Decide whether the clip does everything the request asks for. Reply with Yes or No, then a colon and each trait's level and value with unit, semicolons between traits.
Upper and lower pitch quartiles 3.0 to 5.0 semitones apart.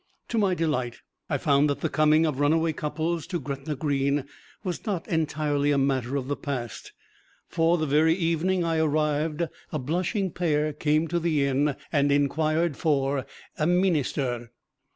No: narrow, 2.6 semitones